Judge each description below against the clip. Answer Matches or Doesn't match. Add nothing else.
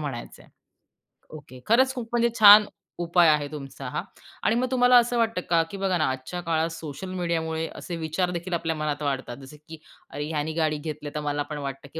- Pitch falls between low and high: Matches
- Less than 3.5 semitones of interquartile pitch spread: Doesn't match